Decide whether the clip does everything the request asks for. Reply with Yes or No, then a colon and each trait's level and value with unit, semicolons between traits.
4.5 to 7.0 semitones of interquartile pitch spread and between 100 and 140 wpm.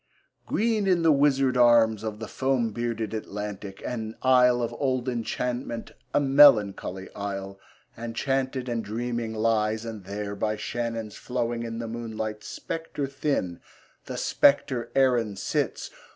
No: average, 3.2 semitones; slow, 135 wpm